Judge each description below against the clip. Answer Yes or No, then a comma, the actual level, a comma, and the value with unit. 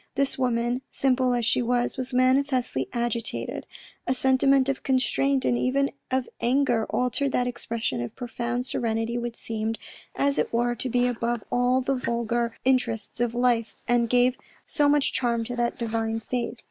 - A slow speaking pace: No, average, 165 wpm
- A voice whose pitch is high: Yes, high, 245 Hz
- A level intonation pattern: Yes, narrow, 1.8 semitones